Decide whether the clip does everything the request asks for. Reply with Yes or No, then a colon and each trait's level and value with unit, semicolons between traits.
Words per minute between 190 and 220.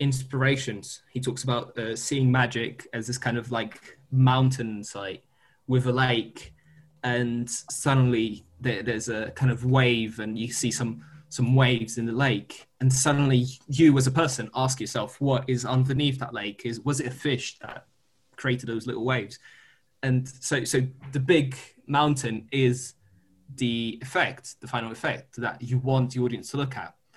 No: average, 170 wpm